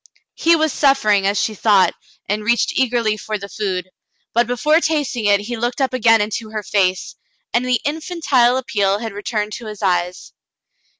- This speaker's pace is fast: No, average, 175 wpm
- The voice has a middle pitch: No, high, 225 Hz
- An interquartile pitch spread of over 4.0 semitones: No, average, 3.7 semitones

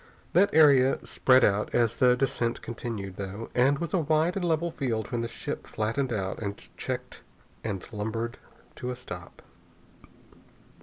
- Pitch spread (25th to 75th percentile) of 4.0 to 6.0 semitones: Yes, average, 4.4 semitones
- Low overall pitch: Yes, low, 120 Hz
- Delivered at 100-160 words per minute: Yes, average, 155 wpm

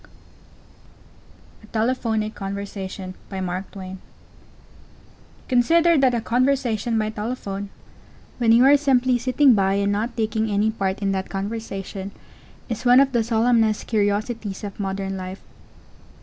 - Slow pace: Yes, slow, 120 wpm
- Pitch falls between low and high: No, high, 220 Hz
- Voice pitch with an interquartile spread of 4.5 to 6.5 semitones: No, average, 3.5 semitones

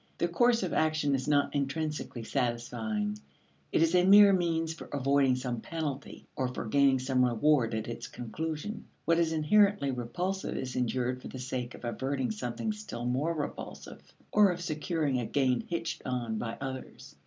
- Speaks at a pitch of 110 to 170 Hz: Yes, medium, 140 Hz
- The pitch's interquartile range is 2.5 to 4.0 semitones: No, average, 4.8 semitones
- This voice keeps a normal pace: Yes, average, 170 wpm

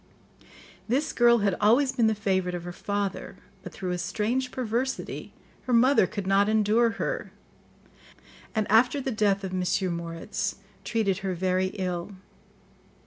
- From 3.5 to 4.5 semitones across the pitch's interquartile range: Yes, average, 4.1 semitones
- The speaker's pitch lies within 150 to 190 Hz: No, high, 205 Hz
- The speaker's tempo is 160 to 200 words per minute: No, average, 145 wpm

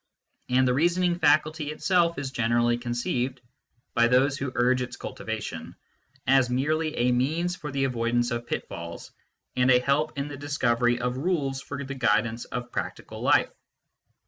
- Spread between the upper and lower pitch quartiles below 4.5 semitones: Yes, average, 3.2 semitones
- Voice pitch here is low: Yes, low, 130 Hz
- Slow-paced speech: No, average, 160 wpm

